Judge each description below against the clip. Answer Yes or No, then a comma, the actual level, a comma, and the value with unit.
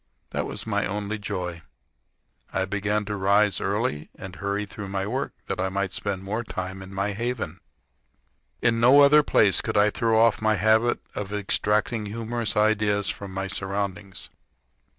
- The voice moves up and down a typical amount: No, narrow, 2.1 semitones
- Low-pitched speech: Yes, low, 105 Hz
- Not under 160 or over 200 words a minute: Yes, average, 165 wpm